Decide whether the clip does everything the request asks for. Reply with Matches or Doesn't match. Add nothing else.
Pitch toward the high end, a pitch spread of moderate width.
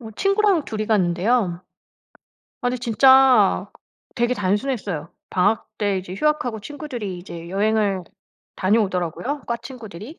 Matches